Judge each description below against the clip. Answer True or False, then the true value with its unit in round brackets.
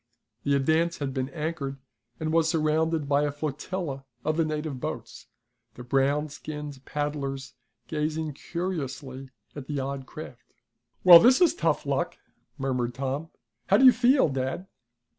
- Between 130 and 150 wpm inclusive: True (145 wpm)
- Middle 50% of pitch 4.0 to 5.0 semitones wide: False (3.0 semitones)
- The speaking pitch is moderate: True (150 Hz)